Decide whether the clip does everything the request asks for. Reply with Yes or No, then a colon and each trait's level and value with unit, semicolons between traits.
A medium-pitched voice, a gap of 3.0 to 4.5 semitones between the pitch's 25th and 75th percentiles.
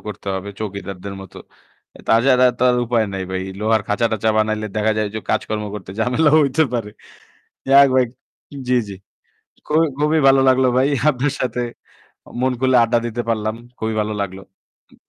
No: low, 115 Hz; average, 3.7 semitones